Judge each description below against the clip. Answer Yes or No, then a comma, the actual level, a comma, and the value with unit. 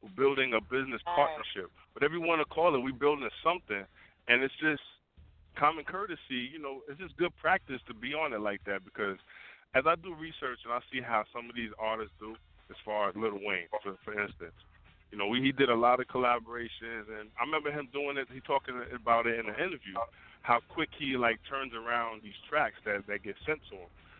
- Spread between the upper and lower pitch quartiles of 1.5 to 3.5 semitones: No, average, 4.6 semitones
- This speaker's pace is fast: Yes, fast, 220 wpm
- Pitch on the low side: Yes, low, 120 Hz